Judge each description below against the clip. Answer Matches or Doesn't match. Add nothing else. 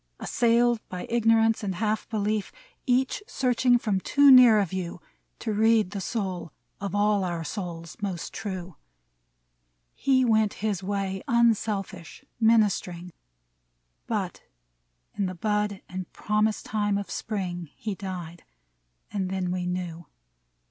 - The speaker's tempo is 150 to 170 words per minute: Doesn't match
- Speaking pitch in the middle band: Doesn't match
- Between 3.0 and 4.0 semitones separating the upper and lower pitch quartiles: Matches